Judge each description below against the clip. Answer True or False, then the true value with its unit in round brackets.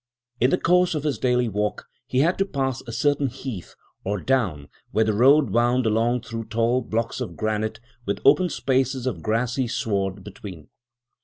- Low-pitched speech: True (120 Hz)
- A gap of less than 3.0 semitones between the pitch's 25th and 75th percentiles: False (3.6 semitones)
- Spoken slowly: False (175 wpm)